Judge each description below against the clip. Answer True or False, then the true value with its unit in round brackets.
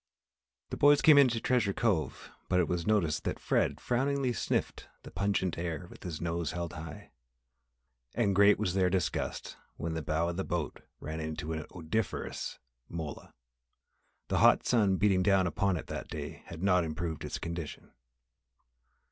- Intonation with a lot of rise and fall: False (4.0 semitones)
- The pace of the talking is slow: False (160 wpm)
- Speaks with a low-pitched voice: True (90 Hz)